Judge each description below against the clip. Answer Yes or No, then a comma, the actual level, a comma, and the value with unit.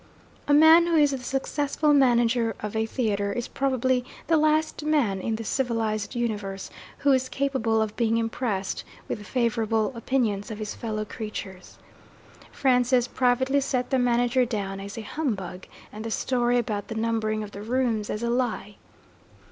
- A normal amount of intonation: Yes, average, 3.4 semitones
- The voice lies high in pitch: Yes, high, 235 Hz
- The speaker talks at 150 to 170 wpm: Yes, average, 165 wpm